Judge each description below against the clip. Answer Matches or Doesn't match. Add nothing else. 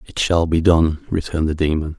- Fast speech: Matches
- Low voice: Matches